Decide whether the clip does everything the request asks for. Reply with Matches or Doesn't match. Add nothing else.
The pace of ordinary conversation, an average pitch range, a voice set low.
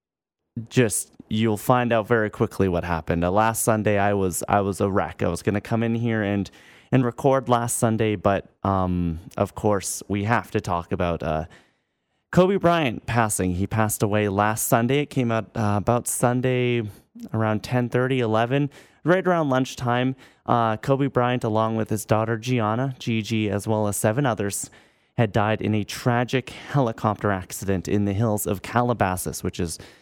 Matches